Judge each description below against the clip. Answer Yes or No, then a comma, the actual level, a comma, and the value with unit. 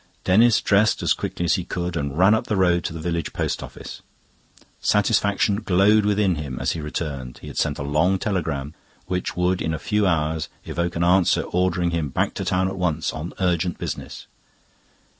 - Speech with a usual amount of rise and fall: Yes, average, 3.3 semitones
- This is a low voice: Yes, very low, 90 Hz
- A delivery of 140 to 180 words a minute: No, average, 195 wpm